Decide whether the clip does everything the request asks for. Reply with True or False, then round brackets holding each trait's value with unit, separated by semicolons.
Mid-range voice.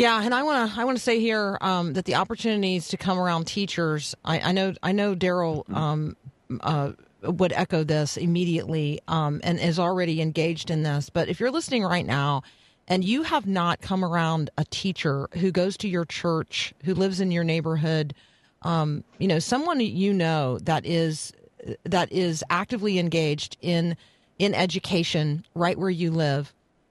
True (170 Hz)